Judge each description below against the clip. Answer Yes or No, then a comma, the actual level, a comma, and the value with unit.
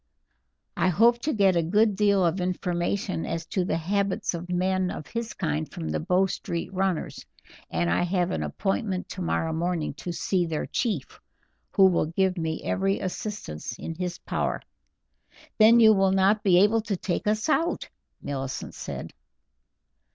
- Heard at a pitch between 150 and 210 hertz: Yes, medium, 185 Hz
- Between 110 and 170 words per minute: Yes, average, 165 wpm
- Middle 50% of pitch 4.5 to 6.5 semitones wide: No, average, 3.1 semitones